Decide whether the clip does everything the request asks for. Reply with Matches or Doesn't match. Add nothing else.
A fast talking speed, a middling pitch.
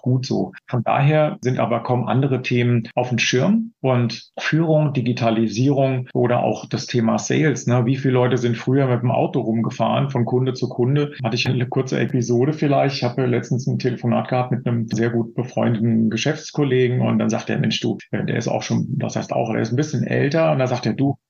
Doesn't match